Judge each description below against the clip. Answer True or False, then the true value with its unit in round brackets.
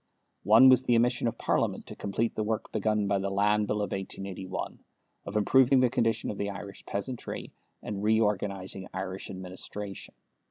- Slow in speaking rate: False (165 wpm)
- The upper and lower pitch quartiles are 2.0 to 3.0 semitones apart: True (2.6 semitones)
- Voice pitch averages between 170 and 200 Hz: False (105 Hz)